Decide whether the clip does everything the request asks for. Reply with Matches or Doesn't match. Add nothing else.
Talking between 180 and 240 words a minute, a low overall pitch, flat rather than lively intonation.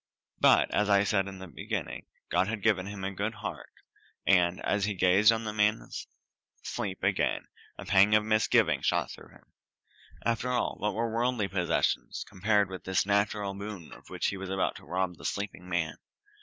Matches